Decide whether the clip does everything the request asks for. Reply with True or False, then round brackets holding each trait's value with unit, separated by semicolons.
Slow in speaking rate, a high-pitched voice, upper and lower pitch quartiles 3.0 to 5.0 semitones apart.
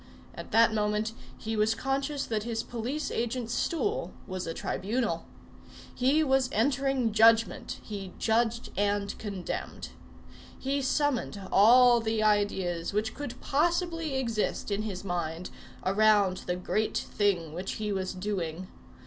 True (130 wpm; 220 Hz; 4.0 semitones)